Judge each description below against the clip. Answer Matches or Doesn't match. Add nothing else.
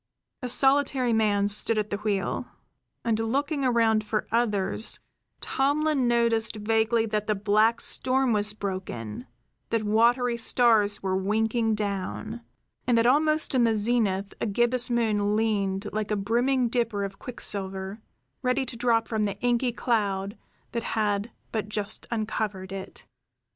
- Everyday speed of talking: Matches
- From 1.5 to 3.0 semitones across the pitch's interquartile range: Matches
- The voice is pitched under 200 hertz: Doesn't match